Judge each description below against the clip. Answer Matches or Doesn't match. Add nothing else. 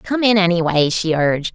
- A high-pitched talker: Doesn't match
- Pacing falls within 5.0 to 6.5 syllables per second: Matches